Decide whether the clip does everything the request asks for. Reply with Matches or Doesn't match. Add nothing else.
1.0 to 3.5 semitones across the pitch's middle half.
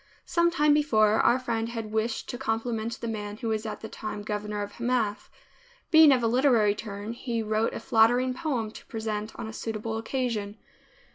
Matches